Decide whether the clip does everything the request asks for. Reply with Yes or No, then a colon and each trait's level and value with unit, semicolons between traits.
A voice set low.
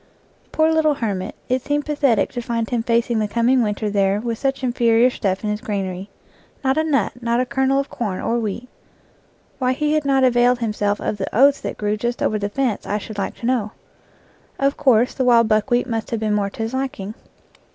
No: high, 235 Hz